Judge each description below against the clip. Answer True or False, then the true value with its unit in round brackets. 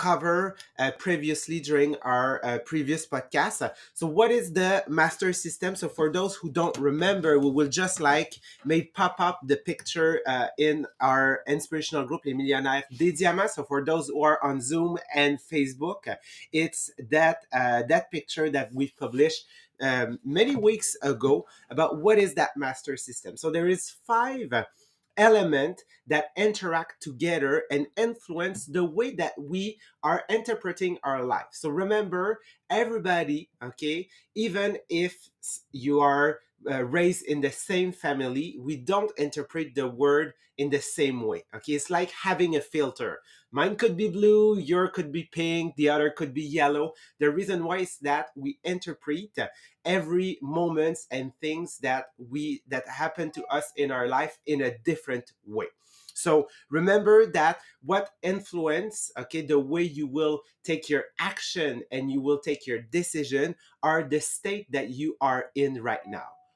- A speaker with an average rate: True (160 wpm)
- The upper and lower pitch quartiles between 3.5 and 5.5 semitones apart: True (4.1 semitones)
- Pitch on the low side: False (160 Hz)